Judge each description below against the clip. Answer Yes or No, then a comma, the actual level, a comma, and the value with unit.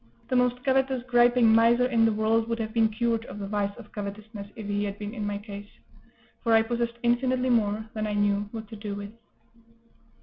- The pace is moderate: No, fast, 210 wpm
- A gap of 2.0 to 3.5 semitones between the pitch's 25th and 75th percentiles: Yes, narrow, 2.6 semitones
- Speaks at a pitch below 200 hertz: No, high, 225 Hz